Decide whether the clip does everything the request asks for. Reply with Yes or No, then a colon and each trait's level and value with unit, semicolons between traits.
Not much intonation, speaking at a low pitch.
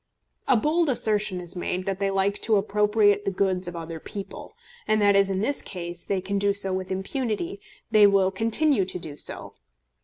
No: narrow, 2.3 semitones; high, 200 Hz